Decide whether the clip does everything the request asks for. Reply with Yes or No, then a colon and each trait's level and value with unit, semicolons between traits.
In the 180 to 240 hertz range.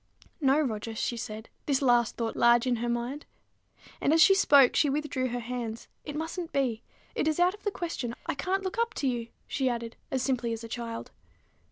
No: very high, 255 Hz